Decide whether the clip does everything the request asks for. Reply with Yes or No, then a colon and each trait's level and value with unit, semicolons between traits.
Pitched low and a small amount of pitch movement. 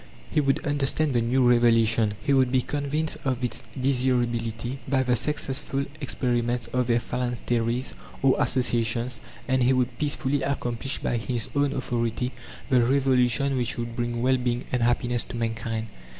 Yes: low, 125 Hz; narrow, 2.0 semitones